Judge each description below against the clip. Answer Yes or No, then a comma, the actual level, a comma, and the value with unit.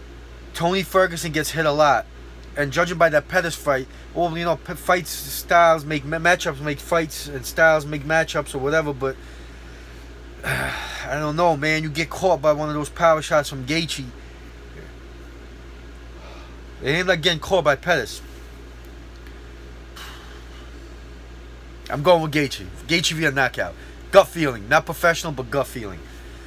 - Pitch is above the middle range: No, medium, 140 Hz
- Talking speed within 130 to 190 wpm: Yes, average, 150 wpm